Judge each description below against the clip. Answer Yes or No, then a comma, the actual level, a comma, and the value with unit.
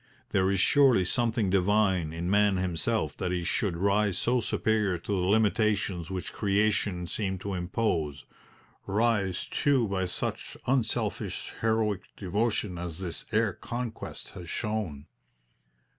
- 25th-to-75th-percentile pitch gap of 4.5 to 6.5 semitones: No, average, 3.3 semitones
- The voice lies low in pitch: Yes, low, 100 Hz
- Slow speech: Yes, slow, 130 wpm